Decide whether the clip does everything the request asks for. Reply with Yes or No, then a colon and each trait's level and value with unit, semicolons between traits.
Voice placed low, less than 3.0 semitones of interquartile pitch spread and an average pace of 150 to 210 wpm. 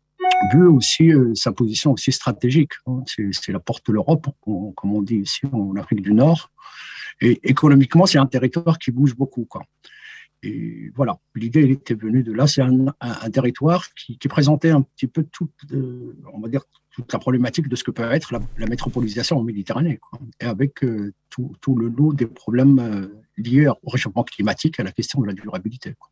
No: low, 130 Hz; average, 3.9 semitones; average, 205 wpm